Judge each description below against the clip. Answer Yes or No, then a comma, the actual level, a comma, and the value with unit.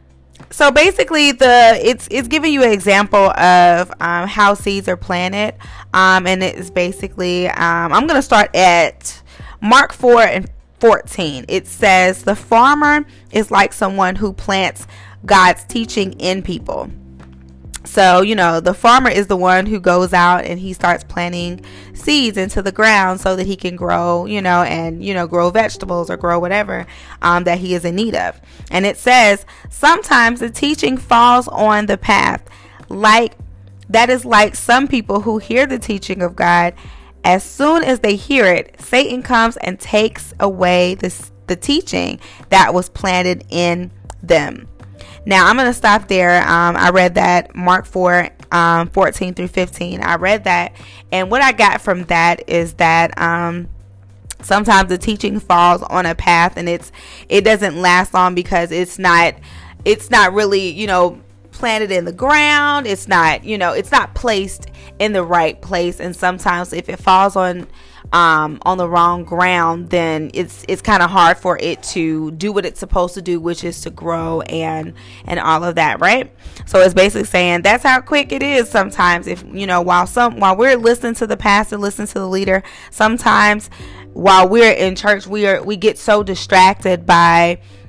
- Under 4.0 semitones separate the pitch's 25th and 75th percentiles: Yes, average, 3.5 semitones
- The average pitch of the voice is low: No, medium, 185 Hz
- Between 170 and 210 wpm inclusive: Yes, average, 180 wpm